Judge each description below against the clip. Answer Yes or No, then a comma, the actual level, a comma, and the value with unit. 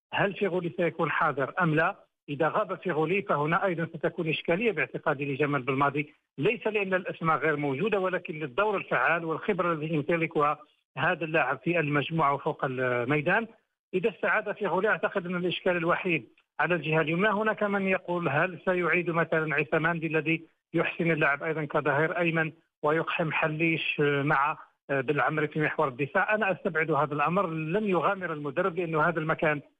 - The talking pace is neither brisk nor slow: No, fast, 145 wpm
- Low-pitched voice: No, medium, 165 Hz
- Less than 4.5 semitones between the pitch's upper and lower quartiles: Yes, average, 2.9 semitones